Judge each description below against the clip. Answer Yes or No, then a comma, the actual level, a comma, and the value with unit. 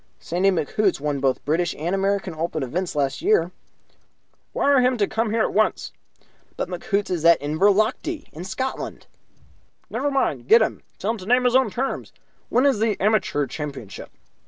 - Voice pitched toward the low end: No, high, 195 Hz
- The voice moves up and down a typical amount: No, wide, 6.3 semitones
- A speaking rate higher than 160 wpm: Yes, average, 170 wpm